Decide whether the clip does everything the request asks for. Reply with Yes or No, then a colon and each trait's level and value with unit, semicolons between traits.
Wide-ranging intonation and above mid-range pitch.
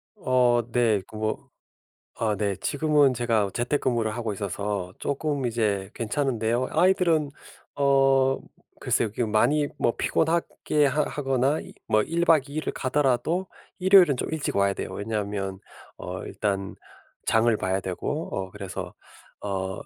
No: wide, 5.7 semitones; low, 120 Hz